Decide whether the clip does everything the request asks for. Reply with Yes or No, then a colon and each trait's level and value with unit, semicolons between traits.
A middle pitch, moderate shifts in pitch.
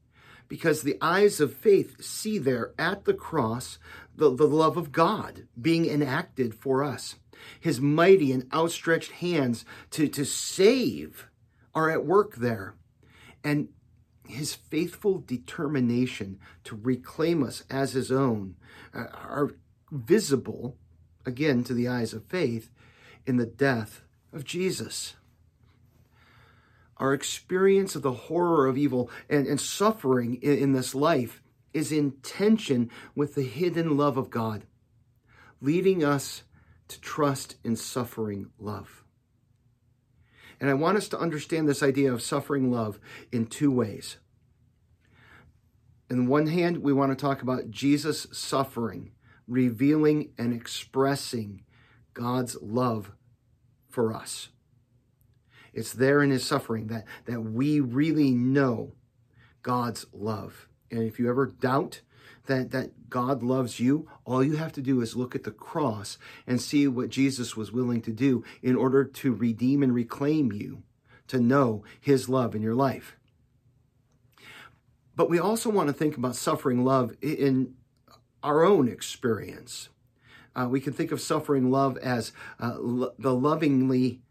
No: low, 125 Hz; average, 3.2 semitones